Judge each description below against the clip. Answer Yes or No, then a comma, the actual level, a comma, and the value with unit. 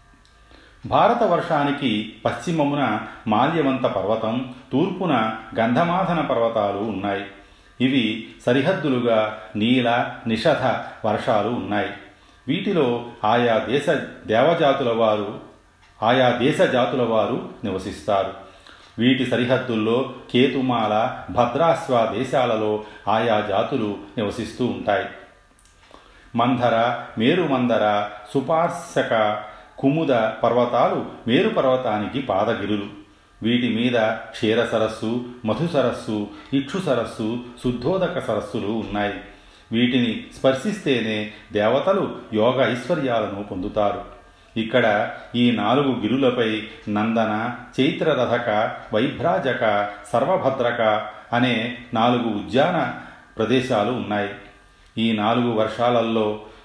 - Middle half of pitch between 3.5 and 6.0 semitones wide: No, average, 2.9 semitones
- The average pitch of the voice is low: Yes, low, 115 Hz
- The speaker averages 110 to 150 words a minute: No, average, 80 wpm